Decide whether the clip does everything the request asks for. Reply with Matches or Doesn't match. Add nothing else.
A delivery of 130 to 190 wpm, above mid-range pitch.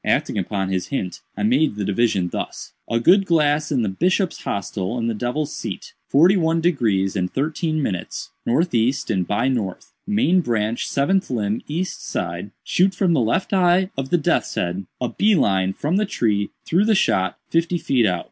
Doesn't match